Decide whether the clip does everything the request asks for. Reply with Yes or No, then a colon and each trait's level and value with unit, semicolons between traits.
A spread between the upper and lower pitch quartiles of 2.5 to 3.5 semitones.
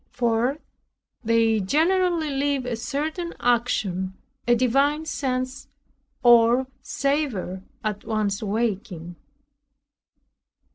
No: average, 4.7 semitones